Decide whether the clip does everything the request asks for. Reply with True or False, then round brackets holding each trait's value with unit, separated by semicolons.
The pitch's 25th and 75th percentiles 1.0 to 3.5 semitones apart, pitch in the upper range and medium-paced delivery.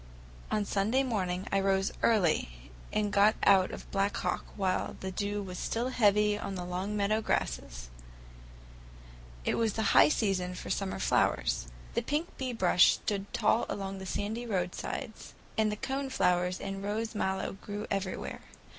True (2.5 semitones; 200 Hz; 160 wpm)